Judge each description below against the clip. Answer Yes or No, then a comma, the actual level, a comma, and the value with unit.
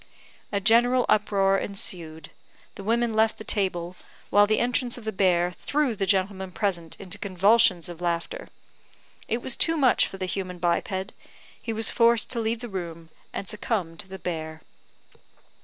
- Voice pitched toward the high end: Yes, high, 195 Hz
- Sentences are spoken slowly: No, average, 165 wpm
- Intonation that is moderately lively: Yes, average, 4.1 semitones